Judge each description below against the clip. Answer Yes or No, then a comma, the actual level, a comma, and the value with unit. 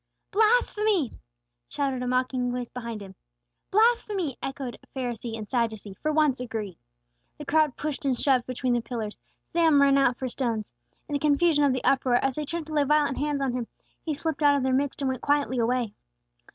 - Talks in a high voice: Yes, very high, 270 Hz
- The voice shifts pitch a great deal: No, average, 3.5 semitones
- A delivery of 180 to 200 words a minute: Yes, average, 190 wpm